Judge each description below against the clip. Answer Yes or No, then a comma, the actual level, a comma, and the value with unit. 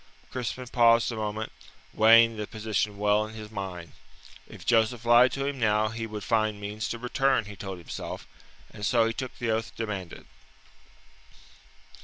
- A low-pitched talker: Yes, low, 110 Hz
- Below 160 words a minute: No, average, 165 wpm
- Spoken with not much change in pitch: Yes, narrow, 1.9 semitones